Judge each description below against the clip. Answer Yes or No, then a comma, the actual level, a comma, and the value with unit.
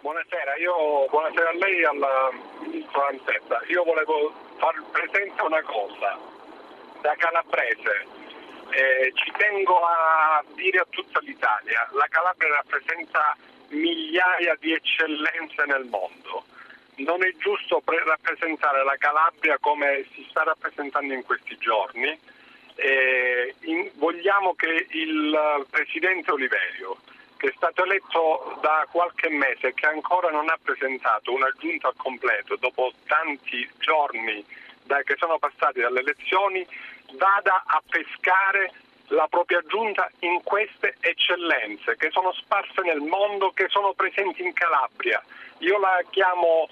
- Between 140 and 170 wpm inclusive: No, average, 130 wpm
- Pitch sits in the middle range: Yes, medium, 170 Hz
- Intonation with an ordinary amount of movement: Yes, average, 4.4 semitones